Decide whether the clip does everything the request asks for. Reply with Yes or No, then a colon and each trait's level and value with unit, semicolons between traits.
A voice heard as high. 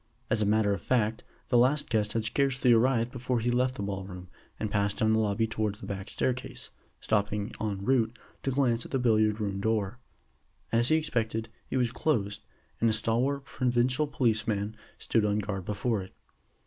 No: low, 110 Hz